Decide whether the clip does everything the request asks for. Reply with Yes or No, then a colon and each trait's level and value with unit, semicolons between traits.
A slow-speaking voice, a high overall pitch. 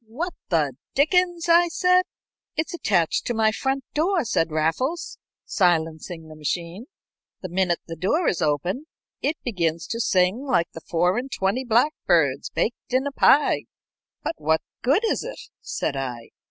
No: average, 155 wpm; high, 215 Hz